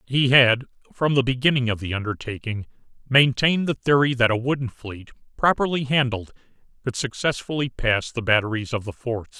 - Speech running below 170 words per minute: Yes, average, 160 wpm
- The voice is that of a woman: No, male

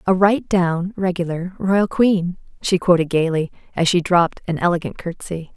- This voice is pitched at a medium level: Yes, medium, 180 Hz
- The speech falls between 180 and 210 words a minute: No, average, 160 wpm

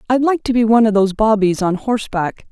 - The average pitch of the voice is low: No, high, 220 Hz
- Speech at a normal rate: No, fast, 240 wpm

